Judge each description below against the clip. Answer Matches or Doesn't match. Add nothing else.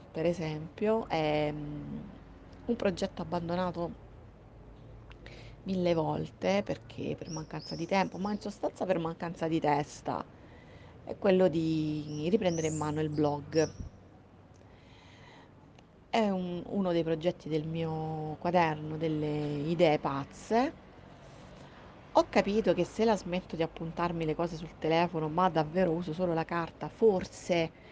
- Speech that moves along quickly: Doesn't match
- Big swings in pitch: Doesn't match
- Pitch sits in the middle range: Matches